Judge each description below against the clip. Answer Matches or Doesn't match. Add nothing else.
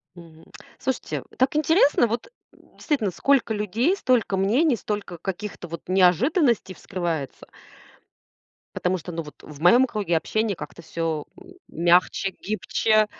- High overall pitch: Matches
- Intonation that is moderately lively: Doesn't match